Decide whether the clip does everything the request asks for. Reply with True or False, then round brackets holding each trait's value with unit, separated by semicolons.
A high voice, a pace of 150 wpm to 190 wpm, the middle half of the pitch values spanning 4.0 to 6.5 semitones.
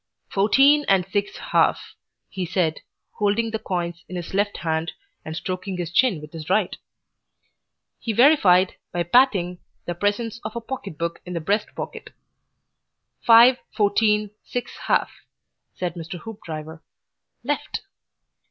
False (195 Hz; 135 wpm; 4.3 semitones)